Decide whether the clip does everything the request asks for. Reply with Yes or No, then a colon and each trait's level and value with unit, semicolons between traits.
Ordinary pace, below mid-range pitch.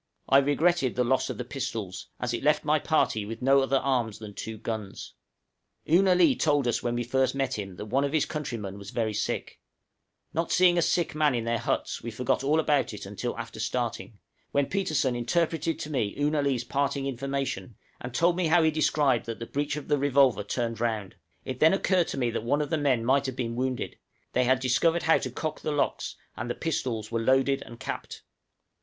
No: fast, 220 wpm; low, 130 Hz